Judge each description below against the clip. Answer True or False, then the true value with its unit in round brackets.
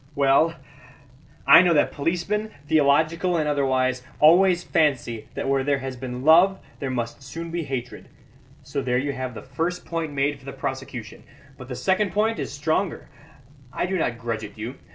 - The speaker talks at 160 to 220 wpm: True (175 wpm)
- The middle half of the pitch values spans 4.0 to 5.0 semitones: True (4.4 semitones)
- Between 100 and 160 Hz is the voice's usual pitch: True (140 Hz)